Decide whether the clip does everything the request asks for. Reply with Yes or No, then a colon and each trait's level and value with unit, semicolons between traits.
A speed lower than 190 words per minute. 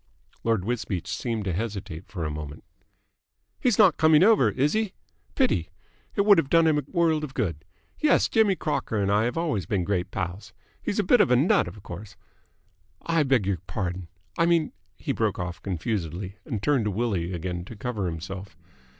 No: average, 195 wpm